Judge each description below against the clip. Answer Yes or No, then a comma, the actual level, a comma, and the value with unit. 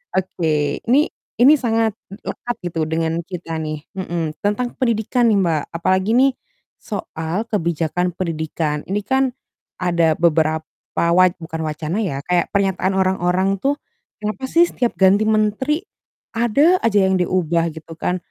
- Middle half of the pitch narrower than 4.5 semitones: No, average, 4.8 semitones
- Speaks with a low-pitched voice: No, medium, 185 Hz